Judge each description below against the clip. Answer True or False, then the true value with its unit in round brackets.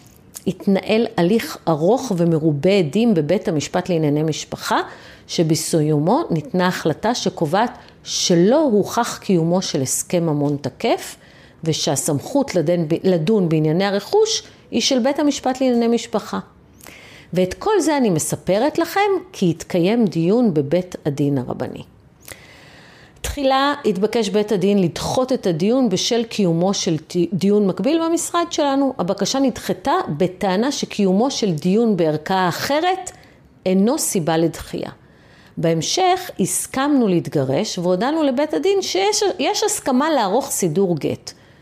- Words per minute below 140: True (115 wpm)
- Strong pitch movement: True (7.6 semitones)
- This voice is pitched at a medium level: False (195 Hz)